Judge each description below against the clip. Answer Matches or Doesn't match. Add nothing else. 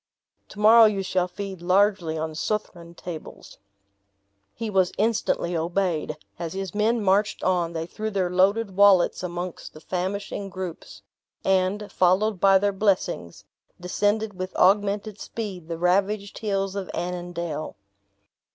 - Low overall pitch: Doesn't match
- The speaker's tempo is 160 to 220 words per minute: Doesn't match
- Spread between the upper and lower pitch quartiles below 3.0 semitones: Matches